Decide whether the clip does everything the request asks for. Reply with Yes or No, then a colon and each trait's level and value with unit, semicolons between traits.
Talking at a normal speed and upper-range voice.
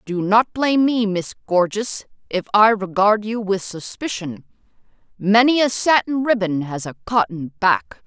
Yes: average, 150 wpm; high, 205 Hz